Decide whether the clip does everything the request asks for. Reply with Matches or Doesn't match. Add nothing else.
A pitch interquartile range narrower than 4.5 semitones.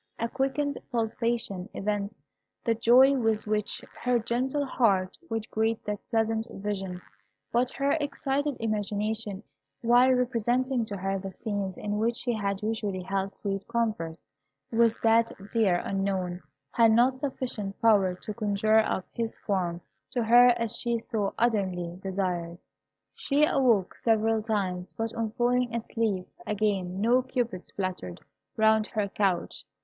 Matches